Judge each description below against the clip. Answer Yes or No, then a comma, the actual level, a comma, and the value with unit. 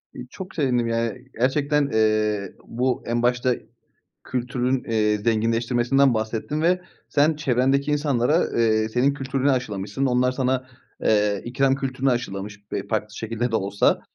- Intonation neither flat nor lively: Yes, average, 3.5 semitones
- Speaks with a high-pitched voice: No, low, 125 Hz